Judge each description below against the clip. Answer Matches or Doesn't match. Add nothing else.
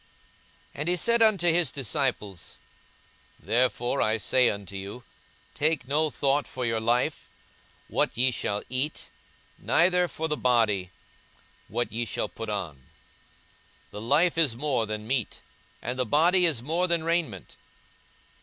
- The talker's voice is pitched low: Matches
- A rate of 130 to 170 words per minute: Matches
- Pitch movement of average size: Doesn't match